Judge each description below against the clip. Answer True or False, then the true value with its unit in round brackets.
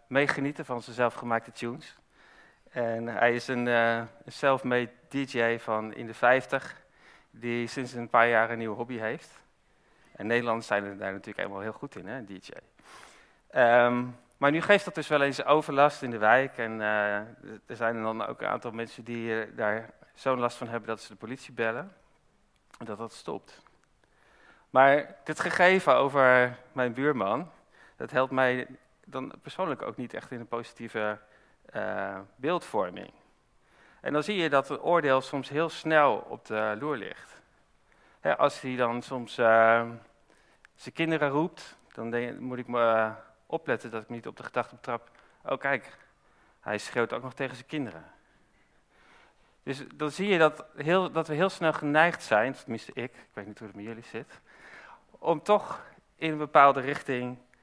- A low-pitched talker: True (125 Hz)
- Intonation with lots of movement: False (3.7 semitones)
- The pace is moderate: True (175 wpm)